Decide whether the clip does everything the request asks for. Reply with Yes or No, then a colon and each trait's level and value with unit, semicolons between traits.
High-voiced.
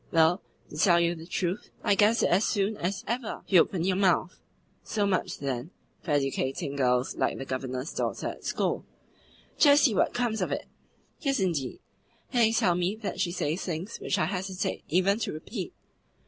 No: medium, 180 Hz